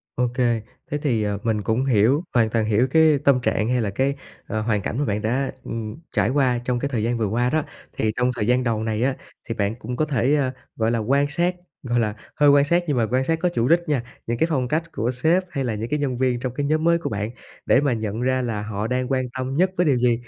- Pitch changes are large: No, average, 3.9 semitones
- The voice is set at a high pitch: No, low, 125 Hz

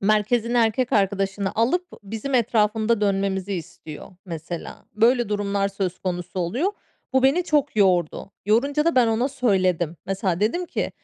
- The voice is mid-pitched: No, high, 210 Hz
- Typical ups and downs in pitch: Yes, average, 4.2 semitones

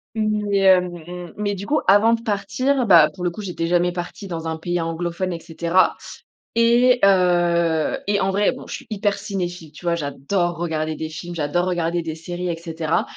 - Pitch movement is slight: No, average, 3.2 semitones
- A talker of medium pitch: Yes, medium, 175 Hz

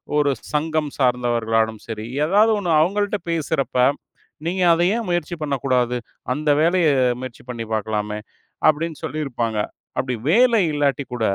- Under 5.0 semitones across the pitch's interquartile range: No, wide, 5.6 semitones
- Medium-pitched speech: Yes, medium, 145 Hz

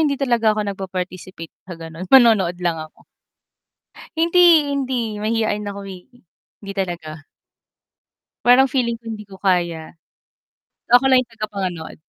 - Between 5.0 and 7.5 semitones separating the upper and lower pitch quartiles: Yes, wide, 5.6 semitones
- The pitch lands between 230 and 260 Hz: No, high, 205 Hz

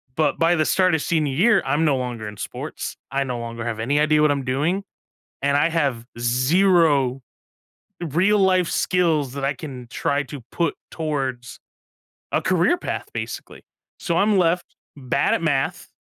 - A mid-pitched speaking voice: Yes, medium, 145 Hz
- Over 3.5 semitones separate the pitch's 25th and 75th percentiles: Yes, average, 4.5 semitones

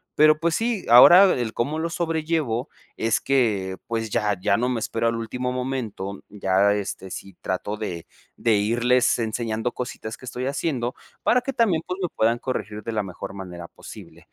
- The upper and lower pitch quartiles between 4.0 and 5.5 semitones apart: Yes, average, 4.7 semitones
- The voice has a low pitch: Yes, low, 115 Hz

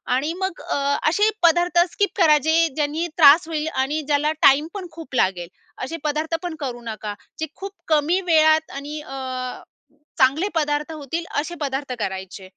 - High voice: Yes, very high, 300 Hz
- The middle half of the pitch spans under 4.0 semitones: Yes, average, 3.4 semitones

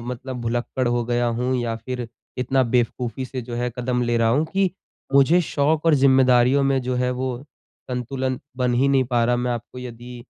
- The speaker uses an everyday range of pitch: No, narrow, 1.6 semitones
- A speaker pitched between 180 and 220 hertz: No, low, 125 Hz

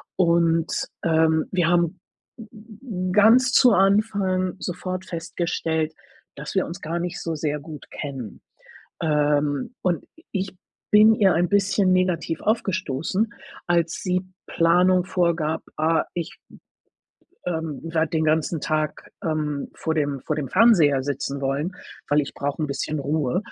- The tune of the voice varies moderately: Yes, average, 3.4 semitones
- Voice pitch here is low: No, medium, 170 Hz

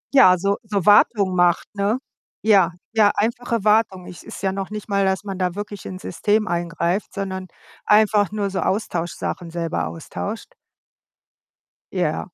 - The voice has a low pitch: No, high, 200 Hz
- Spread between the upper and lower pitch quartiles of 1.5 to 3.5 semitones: Yes, narrow, 2.5 semitones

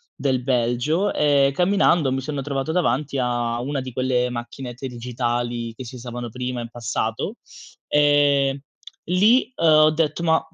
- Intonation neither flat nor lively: Yes, average, 3.5 semitones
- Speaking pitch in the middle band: No, low, 130 Hz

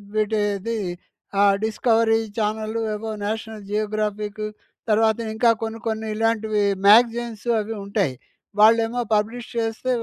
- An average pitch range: No, narrow, 1.1 semitones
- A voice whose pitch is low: No, high, 220 Hz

